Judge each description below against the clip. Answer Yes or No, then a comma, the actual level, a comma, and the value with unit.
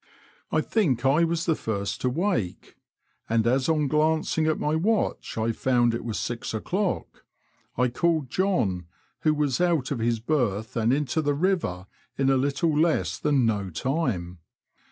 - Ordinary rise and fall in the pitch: No, wide, 5.8 semitones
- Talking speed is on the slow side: No, average, 165 wpm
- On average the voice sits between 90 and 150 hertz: Yes, low, 135 Hz